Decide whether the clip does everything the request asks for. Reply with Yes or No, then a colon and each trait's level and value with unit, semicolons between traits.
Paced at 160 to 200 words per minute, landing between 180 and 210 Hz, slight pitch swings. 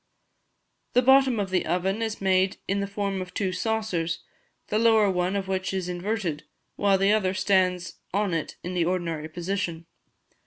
Yes: average, 170 wpm; high, 190 Hz; narrow, 2.3 semitones